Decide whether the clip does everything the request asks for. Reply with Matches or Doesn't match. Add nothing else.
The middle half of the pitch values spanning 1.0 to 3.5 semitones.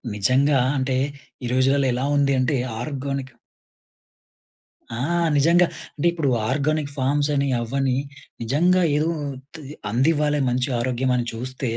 Matches